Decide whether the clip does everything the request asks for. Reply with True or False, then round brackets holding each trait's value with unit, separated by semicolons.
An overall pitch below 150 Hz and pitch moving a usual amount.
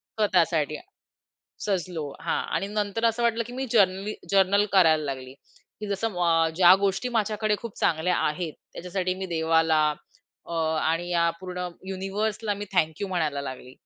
False (185 Hz; 4.1 semitones)